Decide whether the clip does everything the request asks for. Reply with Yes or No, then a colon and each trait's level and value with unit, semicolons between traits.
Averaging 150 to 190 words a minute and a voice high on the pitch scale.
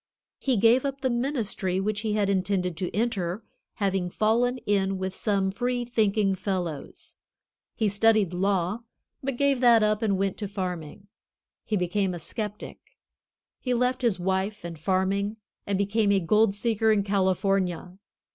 Yes: average, 155 wpm; high, 200 Hz